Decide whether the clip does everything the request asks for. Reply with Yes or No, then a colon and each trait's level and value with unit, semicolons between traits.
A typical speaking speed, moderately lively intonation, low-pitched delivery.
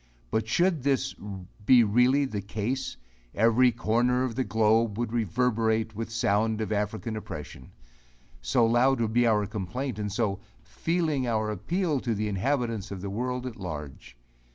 Yes: average, 160 wpm; average, 3.2 semitones; low, 115 Hz